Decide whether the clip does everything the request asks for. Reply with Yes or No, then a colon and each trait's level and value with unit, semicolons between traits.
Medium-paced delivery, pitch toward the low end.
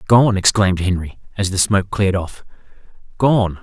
Yes: average, 150 wpm; low, 100 Hz